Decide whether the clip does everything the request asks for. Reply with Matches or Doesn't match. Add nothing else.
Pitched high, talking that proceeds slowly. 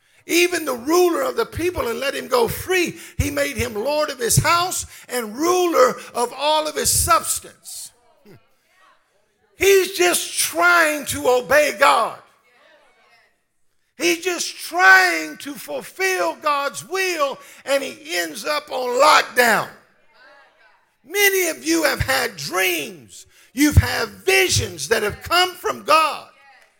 Matches